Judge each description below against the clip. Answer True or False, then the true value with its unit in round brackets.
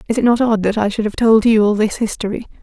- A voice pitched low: False (220 Hz)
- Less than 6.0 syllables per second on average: False (6.5 syllables/s)